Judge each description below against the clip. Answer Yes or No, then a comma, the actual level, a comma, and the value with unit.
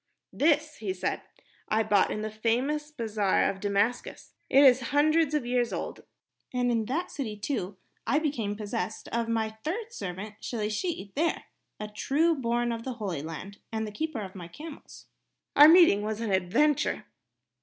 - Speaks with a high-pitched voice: Yes, high, 230 Hz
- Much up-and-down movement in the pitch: Yes, wide, 6.0 semitones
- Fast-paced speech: No, average, 170 wpm